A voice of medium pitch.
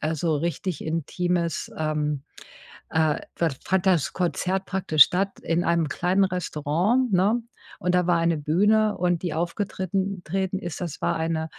Yes: medium, 175 Hz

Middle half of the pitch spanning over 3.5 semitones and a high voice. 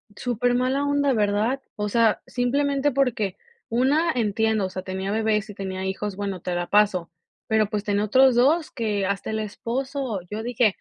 Yes: average, 4.0 semitones; high, 220 Hz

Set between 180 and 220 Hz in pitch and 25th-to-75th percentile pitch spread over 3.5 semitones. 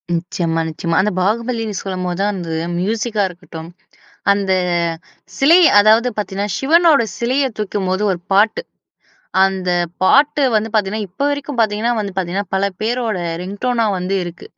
Yes: high, 205 Hz; average, 3.9 semitones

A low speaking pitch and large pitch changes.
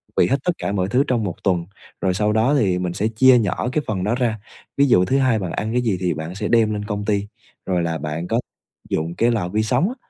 No: low, 105 Hz; average, 4.6 semitones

